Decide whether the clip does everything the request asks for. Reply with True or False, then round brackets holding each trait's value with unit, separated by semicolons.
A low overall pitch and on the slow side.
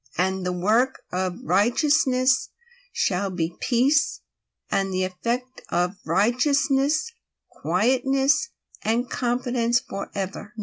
False (240 Hz; 95 wpm)